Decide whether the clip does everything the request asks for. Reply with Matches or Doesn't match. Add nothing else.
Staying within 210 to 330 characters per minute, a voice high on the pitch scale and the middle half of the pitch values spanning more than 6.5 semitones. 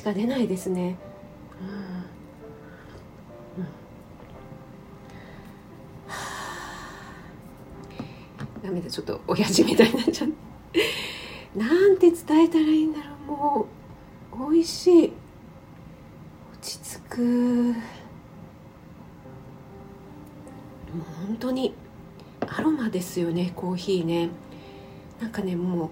Doesn't match